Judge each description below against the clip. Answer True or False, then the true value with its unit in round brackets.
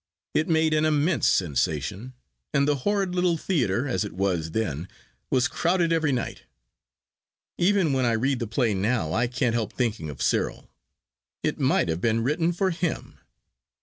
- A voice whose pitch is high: False (125 Hz)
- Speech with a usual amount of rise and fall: False (7.7 semitones)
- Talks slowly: False (165 wpm)